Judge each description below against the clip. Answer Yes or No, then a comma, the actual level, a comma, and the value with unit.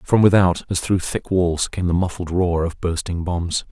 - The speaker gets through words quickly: Yes, fast, 210 wpm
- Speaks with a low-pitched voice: Yes, very low, 90 Hz